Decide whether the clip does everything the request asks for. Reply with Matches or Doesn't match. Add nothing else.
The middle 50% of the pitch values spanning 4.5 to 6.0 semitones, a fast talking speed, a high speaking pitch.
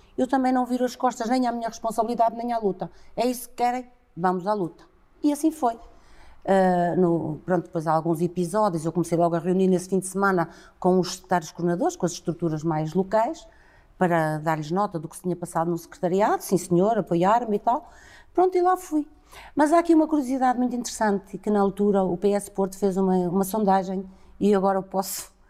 Matches